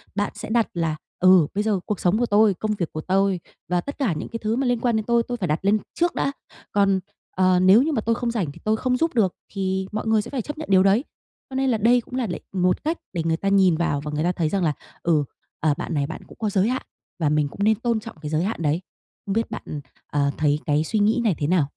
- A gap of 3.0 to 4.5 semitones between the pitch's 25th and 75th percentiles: No, average, 5.1 semitones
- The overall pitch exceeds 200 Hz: No, high, 195 Hz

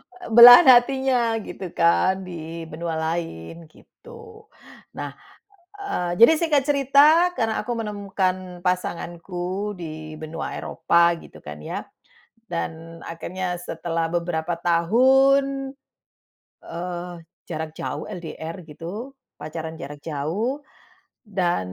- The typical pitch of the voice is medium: Yes, medium, 180 Hz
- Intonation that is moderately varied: No, wide, 6.6 semitones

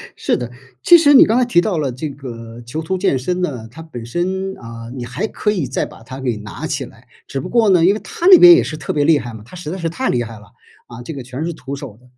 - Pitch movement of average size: No, wide, 7.3 semitones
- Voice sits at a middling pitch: Yes, medium, 145 Hz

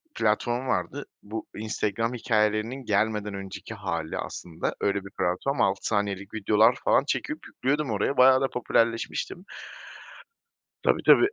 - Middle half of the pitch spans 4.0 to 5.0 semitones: No, average, 3.6 semitones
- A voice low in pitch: Yes, low, 110 Hz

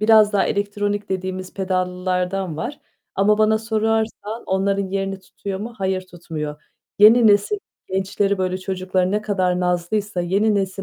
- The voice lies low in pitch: No, high, 195 Hz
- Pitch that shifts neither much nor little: No, narrow, 2.1 semitones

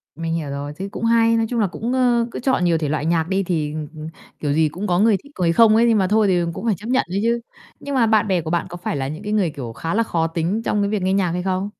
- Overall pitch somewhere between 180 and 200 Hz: Yes, high, 190 Hz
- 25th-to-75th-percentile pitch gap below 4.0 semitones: No, average, 5.3 semitones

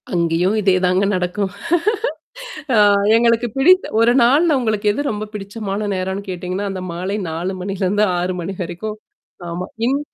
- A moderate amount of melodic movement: Yes, average, 3.1 semitones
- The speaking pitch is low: No, high, 195 Hz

